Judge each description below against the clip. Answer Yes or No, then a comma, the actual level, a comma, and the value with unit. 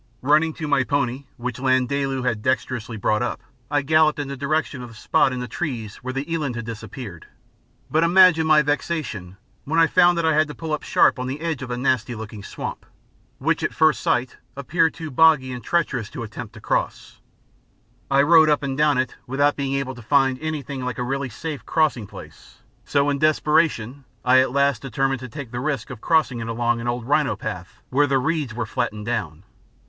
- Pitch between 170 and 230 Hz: No, low, 135 Hz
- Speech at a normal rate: No, fast, 210 wpm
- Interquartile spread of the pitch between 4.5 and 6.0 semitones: No, average, 3.8 semitones